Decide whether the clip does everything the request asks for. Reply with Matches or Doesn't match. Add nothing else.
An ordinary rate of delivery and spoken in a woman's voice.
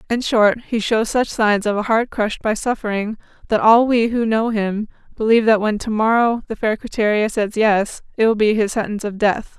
Doesn't match